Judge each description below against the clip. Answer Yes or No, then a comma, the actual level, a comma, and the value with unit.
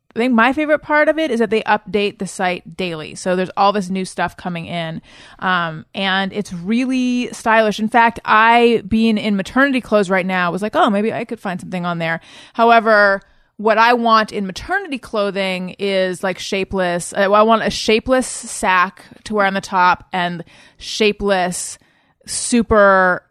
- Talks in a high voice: Yes, high, 205 Hz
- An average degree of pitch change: Yes, average, 3.5 semitones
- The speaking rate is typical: Yes, average, 180 wpm